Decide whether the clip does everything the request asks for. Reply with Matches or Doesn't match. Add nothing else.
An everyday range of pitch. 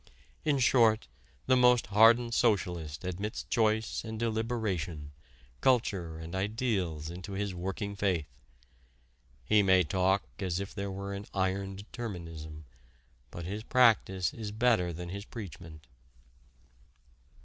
Matches